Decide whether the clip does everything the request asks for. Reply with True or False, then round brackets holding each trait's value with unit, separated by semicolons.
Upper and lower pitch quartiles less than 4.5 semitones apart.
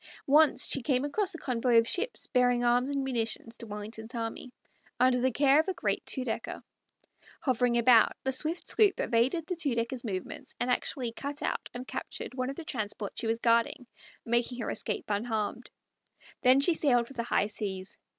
True (3.1 semitones)